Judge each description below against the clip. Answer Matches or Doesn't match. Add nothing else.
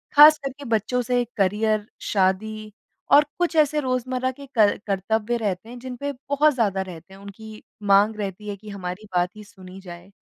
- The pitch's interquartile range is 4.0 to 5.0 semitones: Matches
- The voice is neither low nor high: Doesn't match